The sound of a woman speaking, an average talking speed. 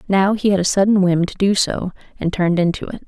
No: female; fast, 255 wpm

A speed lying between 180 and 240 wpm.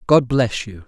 Yes: fast, 205 wpm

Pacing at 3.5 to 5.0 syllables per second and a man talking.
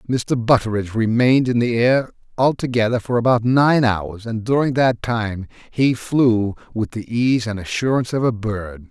Yes: 4.7 syllables/s; male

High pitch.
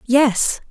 Yes: high, 245 Hz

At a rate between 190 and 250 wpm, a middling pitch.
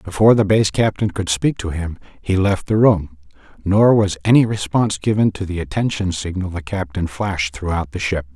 No: average, 195 wpm; very low, 95 Hz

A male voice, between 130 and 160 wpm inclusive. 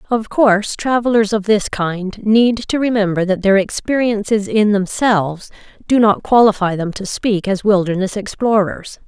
No: female; average, 150 wpm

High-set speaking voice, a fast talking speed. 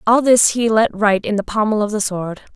Yes: high, 215 Hz; fast, 260 wpm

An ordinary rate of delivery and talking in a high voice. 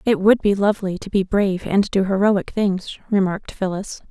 Yes: average, 190 wpm; high, 195 Hz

